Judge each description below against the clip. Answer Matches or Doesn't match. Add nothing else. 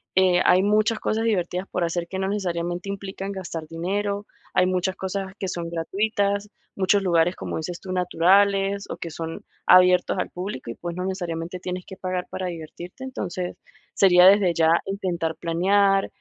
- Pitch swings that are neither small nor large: Doesn't match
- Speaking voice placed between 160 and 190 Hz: Matches